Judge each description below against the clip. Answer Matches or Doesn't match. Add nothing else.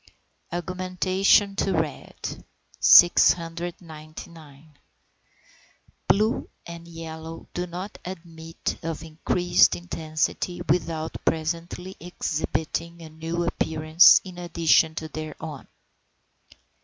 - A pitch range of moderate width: Doesn't match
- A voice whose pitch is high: Doesn't match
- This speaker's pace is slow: Matches